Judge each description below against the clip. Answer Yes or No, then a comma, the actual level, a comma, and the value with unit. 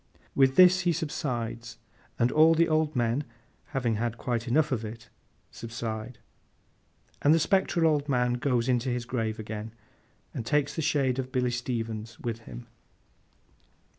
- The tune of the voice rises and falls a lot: No, average, 4.2 semitones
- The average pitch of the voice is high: No, low, 125 Hz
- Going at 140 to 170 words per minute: Yes, average, 150 wpm